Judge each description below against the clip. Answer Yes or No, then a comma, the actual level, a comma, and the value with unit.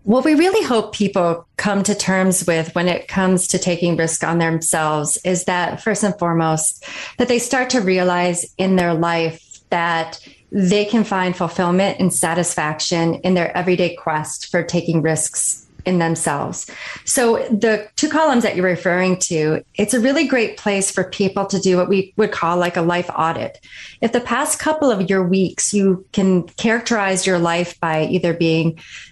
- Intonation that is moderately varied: Yes, average, 3.5 semitones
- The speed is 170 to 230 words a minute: Yes, average, 175 wpm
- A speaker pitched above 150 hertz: Yes, medium, 185 Hz